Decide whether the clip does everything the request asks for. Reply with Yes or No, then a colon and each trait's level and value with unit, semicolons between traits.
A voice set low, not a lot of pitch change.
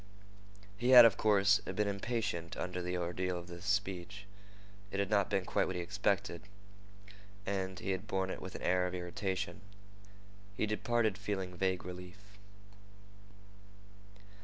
Yes: very low, 95 Hz; narrow, 2.1 semitones